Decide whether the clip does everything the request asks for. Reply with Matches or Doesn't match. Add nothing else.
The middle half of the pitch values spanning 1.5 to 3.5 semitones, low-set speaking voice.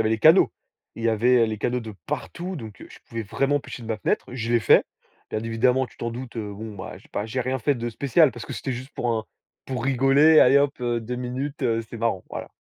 Matches